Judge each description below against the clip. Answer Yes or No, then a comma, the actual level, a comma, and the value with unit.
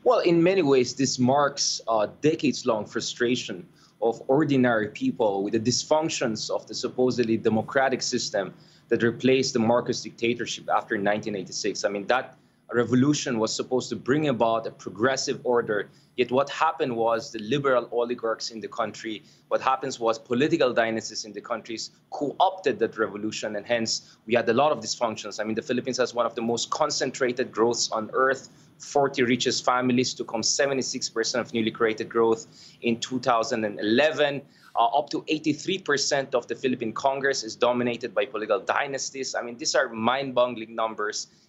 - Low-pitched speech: Yes, low, 120 Hz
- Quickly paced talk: No, average, 165 wpm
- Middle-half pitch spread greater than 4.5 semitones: No, average, 2.9 semitones